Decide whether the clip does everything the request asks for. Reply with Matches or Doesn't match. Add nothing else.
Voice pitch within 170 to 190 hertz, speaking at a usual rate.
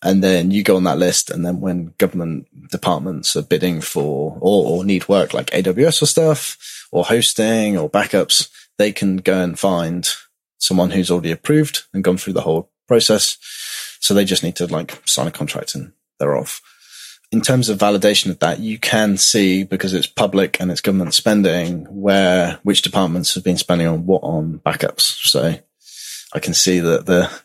Doesn't match